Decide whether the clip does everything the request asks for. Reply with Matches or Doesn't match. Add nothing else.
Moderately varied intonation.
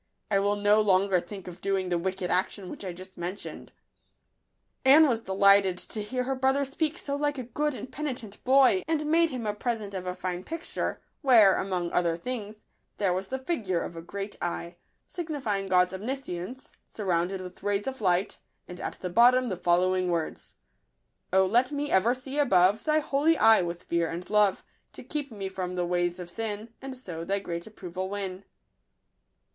Doesn't match